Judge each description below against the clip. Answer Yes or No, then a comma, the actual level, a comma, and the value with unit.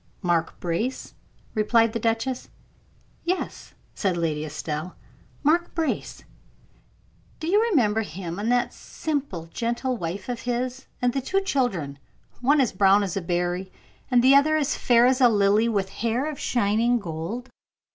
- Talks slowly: No, average, 150 wpm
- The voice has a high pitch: Yes, high, 230 Hz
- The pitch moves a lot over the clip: Yes, wide, 5.7 semitones